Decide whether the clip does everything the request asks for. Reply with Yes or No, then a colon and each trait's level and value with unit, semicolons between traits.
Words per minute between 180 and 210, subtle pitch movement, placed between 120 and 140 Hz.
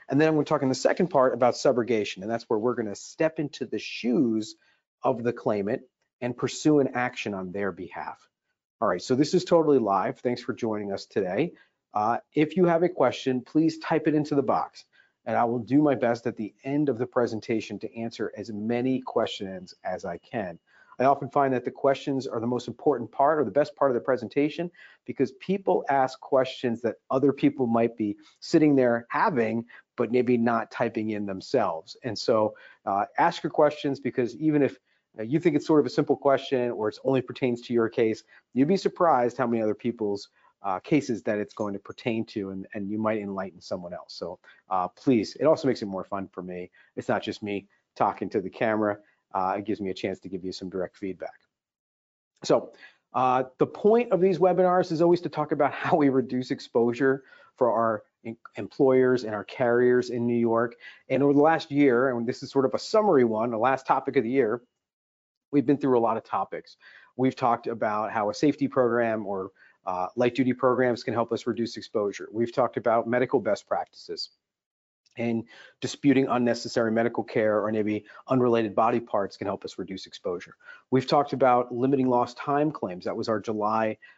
No: fast, 205 wpm; average, 4.1 semitones; low, 125 Hz